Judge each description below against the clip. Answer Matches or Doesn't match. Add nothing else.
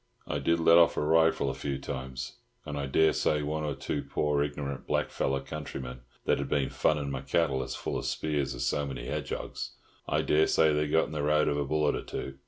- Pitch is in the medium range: Doesn't match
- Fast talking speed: Matches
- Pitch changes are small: Matches